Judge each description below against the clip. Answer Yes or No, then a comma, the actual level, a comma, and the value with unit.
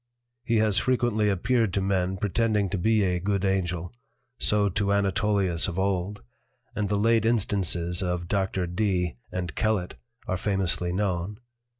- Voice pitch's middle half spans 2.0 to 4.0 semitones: Yes, average, 2.7 semitones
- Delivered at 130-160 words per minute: Yes, average, 150 wpm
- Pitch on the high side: No, low, 100 Hz